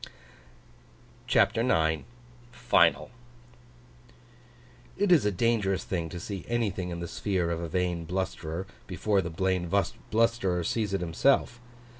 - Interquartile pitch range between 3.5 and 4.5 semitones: Yes, average, 4.0 semitones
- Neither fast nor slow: No, slow, 125 wpm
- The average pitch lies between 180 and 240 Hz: No, very low, 95 Hz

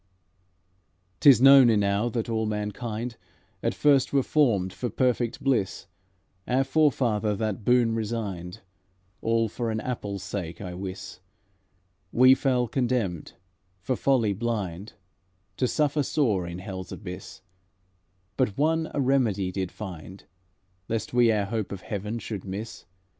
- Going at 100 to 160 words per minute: Yes, slow, 135 wpm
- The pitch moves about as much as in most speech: Yes, average, 4.2 semitones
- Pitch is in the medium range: No, low, 110 Hz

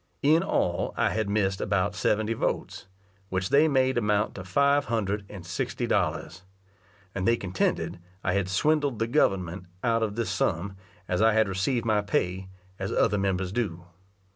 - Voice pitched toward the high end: No, low, 105 Hz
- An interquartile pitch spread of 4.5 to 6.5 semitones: No, average, 3.7 semitones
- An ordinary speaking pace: Yes, average, 165 wpm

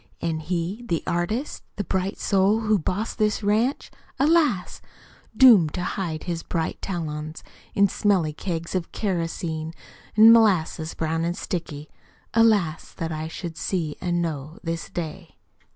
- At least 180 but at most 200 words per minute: No, average, 140 wpm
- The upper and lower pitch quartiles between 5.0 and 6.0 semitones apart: No, average, 4.0 semitones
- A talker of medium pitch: Yes, medium, 175 Hz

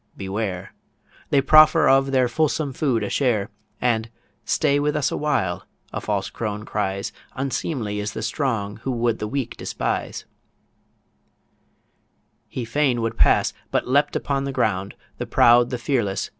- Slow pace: No, average, 150 wpm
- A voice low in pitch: Yes, low, 120 Hz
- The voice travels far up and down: No, average, 4.7 semitones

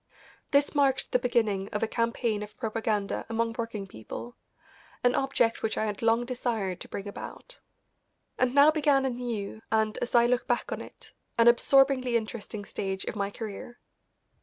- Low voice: No, high, 230 Hz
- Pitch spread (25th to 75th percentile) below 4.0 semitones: Yes, average, 2.8 semitones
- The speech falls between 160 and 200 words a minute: Yes, average, 170 wpm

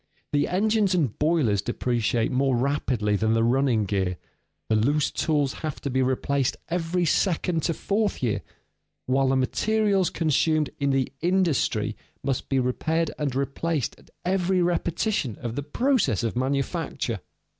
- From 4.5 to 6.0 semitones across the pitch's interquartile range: Yes, average, 5.3 semitones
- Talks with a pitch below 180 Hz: Yes, medium, 140 Hz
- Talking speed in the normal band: Yes, average, 145 wpm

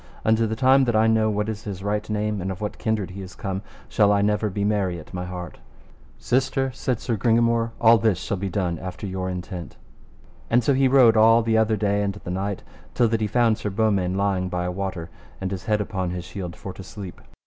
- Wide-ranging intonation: No, average, 3.1 semitones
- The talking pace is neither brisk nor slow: No, fast, 235 wpm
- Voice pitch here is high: No, low, 105 Hz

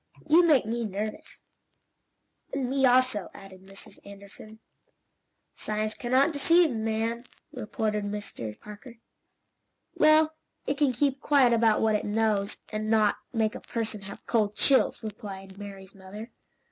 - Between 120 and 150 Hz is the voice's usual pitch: No, high, 220 Hz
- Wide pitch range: No, average, 3.8 semitones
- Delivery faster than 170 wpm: No, slow, 135 wpm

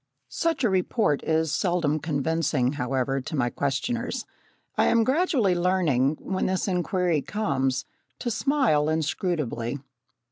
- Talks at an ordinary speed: No, slow, 120 wpm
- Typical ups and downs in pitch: No, wide, 6.2 semitones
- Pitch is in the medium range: Yes, medium, 160 Hz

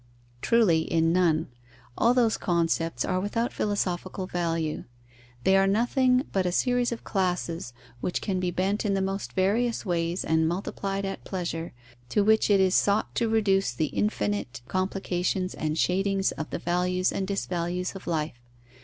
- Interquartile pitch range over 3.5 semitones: No, average, 3.0 semitones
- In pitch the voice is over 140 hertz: Yes, medium, 185 Hz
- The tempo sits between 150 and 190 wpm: Yes, average, 160 wpm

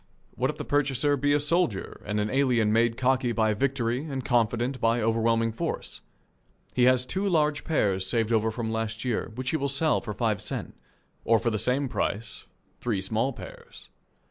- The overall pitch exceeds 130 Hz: No, low, 120 Hz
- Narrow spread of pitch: No, average, 3.5 semitones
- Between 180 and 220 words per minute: Yes, average, 185 wpm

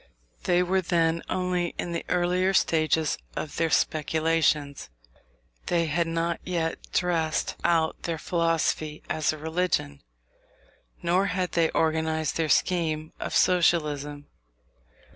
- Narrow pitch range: Yes, narrow, 1.9 semitones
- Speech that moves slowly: Yes, slow, 120 wpm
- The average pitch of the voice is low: No, medium, 165 Hz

